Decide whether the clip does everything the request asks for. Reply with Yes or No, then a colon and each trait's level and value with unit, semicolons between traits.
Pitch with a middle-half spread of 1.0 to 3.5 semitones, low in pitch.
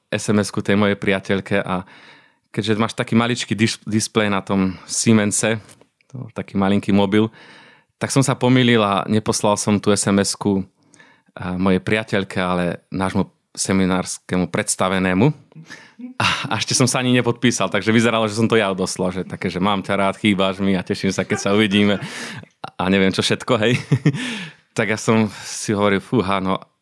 Yes: average, 2.8 semitones; low, 105 Hz